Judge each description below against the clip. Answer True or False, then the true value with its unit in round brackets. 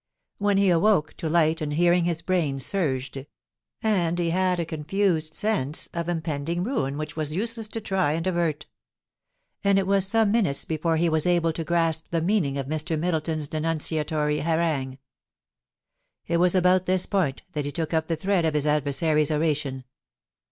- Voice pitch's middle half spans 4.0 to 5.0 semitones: False (3.2 semitones)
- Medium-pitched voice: True (165 Hz)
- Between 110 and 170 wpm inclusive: False (180 wpm)